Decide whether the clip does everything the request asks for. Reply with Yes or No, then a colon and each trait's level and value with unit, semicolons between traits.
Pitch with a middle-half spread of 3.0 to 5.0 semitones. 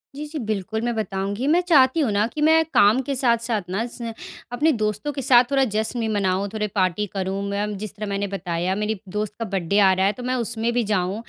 Yes: average, 3.6 semitones